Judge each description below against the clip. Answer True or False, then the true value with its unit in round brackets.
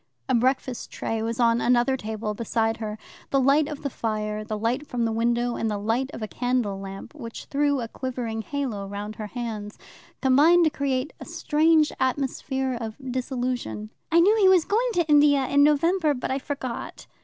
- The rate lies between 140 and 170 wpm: False (190 wpm)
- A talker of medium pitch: False (250 Hz)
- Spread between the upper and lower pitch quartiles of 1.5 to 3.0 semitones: False (4.3 semitones)